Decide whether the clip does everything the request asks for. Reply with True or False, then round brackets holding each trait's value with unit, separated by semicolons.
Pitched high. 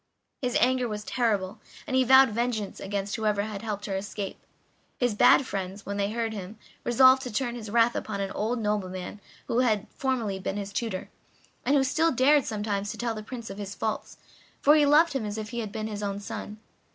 True (215 Hz)